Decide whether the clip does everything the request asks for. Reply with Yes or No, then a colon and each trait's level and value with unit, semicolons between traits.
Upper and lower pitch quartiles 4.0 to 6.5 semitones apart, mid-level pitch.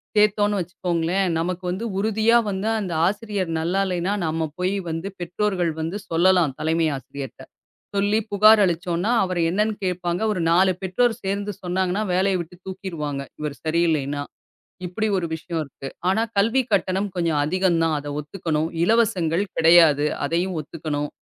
No: average, 3.4 semitones; medium, 180 Hz